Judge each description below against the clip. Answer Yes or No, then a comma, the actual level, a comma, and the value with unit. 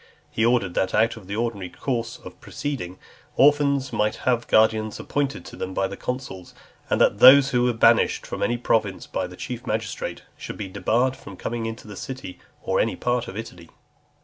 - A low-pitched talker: Yes, low, 115 Hz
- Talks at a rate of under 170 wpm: No, average, 190 wpm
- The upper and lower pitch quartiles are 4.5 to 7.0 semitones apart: No, average, 3.7 semitones